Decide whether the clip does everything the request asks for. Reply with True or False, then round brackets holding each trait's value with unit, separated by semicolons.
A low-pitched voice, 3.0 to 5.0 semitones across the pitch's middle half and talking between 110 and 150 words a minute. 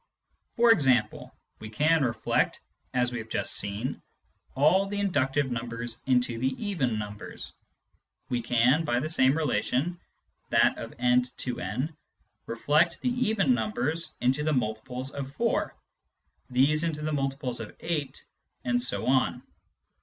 True (130 Hz; 4.3 semitones; 140 wpm)